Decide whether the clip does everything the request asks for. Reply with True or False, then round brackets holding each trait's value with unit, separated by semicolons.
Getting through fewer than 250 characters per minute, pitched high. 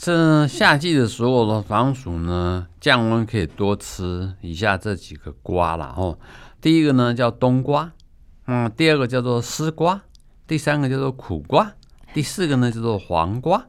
False (235 characters per minute; 120 Hz)